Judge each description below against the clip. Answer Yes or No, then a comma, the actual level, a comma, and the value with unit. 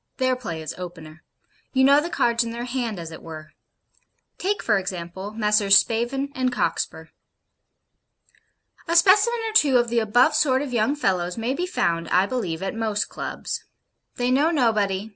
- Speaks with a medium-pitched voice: No, high, 230 Hz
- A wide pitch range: Yes, wide, 5.8 semitones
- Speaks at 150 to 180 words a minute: Yes, average, 170 wpm